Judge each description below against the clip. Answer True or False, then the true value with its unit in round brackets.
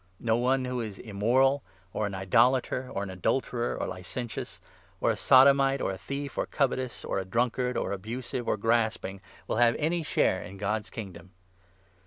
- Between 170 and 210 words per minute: True (180 wpm)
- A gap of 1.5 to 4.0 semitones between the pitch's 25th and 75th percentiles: False (4.5 semitones)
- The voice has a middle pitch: False (120 Hz)